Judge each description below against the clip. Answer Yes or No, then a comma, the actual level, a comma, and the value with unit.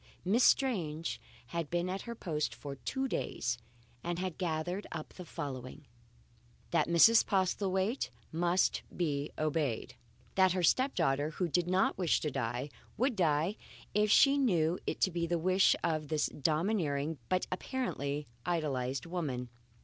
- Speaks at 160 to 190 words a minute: No, average, 150 wpm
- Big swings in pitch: No, average, 4.0 semitones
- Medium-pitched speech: Yes, medium, 170 Hz